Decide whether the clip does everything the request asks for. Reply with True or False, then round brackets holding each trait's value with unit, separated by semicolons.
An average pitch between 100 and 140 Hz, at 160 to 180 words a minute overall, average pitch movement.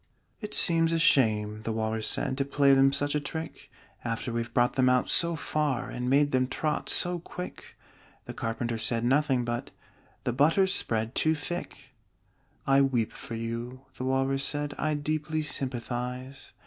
True (135 Hz; 165 wpm; 3.8 semitones)